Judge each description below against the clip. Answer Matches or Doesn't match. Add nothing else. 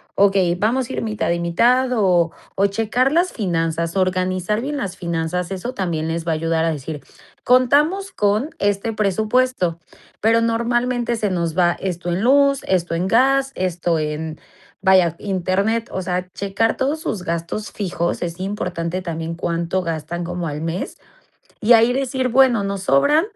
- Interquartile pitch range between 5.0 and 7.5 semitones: Matches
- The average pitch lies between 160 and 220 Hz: Matches